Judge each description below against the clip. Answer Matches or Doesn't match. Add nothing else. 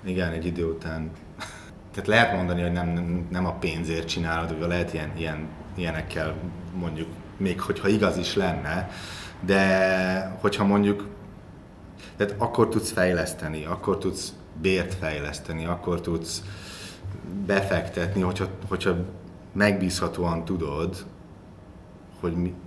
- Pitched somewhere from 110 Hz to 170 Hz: Doesn't match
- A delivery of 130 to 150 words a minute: Doesn't match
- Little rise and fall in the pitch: Matches